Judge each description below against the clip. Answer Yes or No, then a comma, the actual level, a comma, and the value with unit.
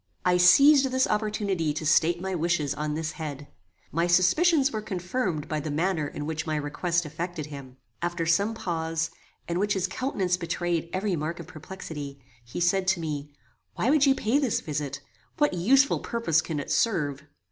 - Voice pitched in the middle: Yes, medium, 175 Hz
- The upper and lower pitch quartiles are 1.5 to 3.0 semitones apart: No, average, 4.4 semitones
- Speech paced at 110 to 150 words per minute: No, average, 180 wpm